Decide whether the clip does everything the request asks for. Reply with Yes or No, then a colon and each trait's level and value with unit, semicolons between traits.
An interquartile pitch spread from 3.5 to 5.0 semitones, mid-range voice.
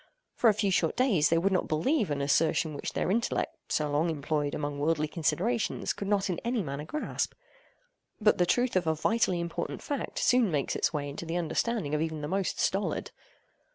No: wide, 5.6 semitones; medium, 170 Hz